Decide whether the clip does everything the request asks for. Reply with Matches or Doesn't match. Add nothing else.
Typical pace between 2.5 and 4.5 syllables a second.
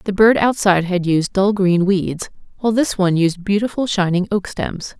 Doesn't match